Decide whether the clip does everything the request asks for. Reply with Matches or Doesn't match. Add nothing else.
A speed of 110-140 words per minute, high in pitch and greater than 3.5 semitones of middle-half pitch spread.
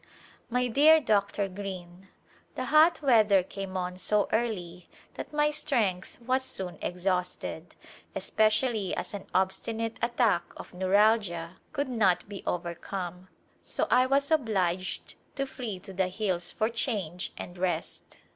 Matches